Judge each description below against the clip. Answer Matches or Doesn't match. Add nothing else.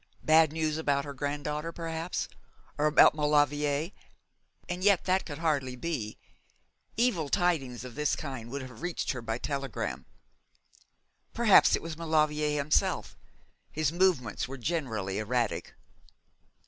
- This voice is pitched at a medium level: Matches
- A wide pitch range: Doesn't match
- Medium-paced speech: Doesn't match